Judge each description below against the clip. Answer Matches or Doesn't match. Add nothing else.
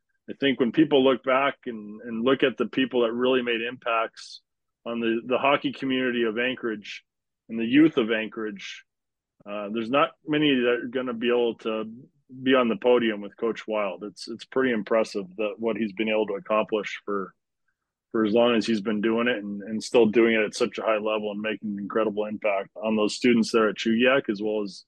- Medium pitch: Doesn't match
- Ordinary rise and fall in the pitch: Doesn't match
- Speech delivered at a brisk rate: Matches